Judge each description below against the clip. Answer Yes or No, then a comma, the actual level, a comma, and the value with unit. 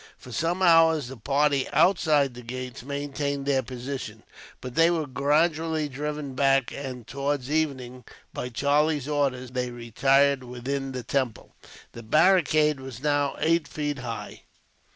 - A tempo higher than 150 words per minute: No, average, 140 wpm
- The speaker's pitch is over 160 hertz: No, medium, 140 Hz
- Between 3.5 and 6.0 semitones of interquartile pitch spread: No, average, 2.8 semitones